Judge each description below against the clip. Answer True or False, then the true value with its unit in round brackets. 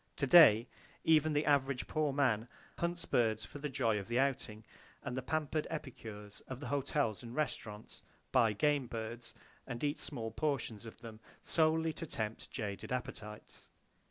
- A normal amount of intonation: True (4.8 semitones)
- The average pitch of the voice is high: False (125 Hz)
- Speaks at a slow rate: False (160 wpm)